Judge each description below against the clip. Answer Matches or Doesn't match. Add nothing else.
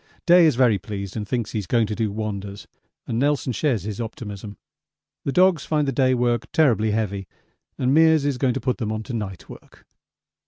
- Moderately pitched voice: Doesn't match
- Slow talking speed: Doesn't match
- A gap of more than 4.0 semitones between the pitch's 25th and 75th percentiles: Matches